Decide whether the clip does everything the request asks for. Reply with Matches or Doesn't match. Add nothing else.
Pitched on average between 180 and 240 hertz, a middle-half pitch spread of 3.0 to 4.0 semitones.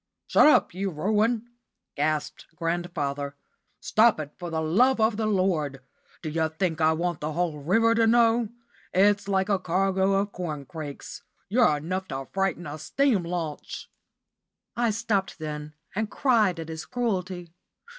Doesn't match